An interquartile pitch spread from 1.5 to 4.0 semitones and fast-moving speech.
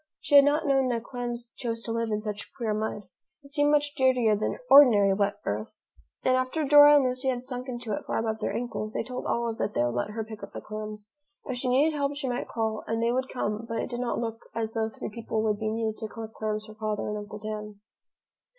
Yes: average, 3.1 semitones; fast, 250 wpm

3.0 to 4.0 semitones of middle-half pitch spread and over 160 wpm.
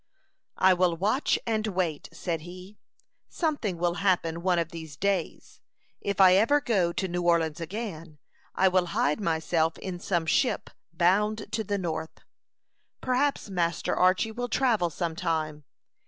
No: average, 3.7 semitones; average, 150 wpm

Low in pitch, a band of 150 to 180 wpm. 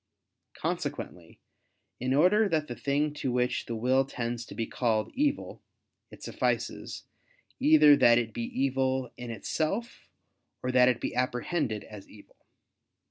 No: low, 130 Hz; slow, 135 wpm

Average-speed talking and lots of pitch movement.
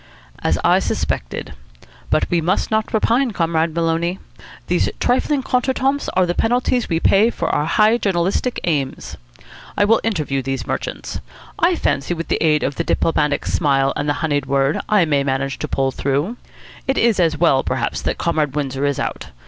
Yes: average, 180 wpm; wide, 7.2 semitones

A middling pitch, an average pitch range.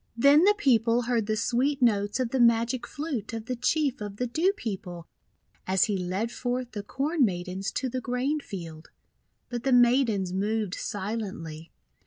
No: high, 230 Hz; average, 4.2 semitones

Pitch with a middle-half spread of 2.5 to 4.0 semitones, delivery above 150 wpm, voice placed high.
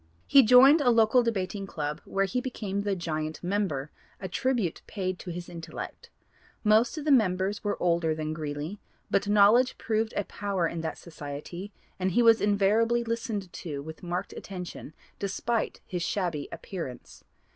No: average, 4.7 semitones; average, 160 wpm; high, 195 Hz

